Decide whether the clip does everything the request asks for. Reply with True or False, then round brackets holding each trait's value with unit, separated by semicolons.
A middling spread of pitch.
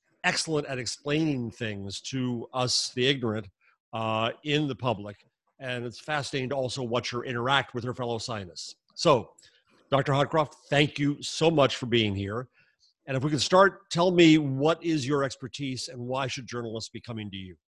True (3.6 semitones)